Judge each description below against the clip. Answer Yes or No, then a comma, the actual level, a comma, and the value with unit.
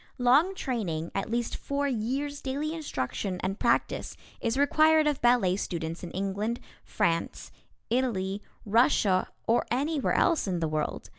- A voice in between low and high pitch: No, high, 235 Hz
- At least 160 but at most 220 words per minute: No, average, 140 wpm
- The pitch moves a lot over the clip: Yes, wide, 6.9 semitones